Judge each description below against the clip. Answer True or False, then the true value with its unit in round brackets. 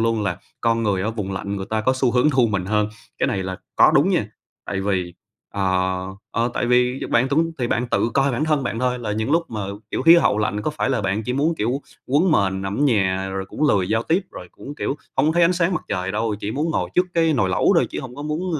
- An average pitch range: False (6.2 semitones)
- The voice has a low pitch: True (115 Hz)